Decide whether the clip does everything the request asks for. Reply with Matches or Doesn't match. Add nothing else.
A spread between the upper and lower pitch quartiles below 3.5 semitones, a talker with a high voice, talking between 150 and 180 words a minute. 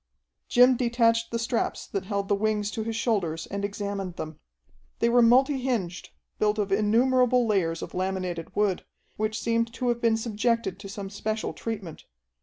Matches